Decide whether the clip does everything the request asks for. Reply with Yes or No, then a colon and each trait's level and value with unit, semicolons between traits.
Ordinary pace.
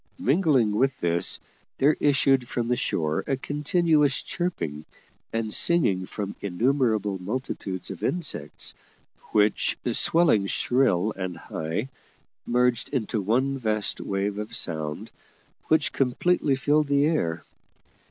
No: slow, 115 wpm